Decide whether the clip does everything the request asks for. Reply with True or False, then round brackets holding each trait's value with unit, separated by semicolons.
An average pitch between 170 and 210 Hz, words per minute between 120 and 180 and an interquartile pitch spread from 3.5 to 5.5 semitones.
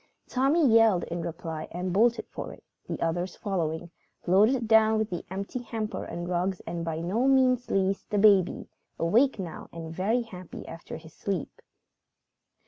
True (190 Hz; 160 wpm; 4.7 semitones)